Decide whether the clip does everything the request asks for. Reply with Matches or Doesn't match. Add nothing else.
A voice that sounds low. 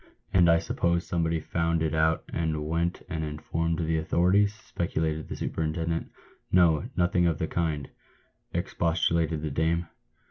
Matches